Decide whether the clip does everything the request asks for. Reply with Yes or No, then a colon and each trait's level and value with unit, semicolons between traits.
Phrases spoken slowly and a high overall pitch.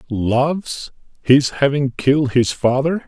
No: slow, 115 wpm; low, 135 Hz